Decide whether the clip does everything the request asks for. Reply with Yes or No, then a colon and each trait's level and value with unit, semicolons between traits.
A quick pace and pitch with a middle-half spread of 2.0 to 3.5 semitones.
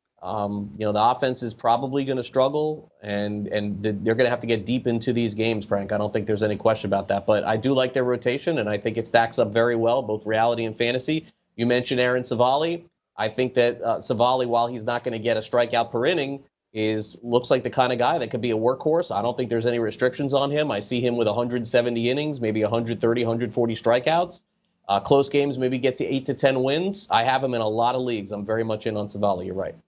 Yes: fast, 250 wpm; average, 2.8 semitones